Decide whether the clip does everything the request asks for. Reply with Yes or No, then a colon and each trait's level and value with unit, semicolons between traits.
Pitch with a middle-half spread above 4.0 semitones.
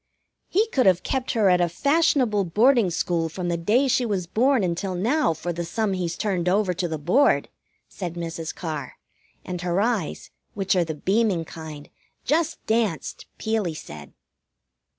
Yes: average, 5.1 semitones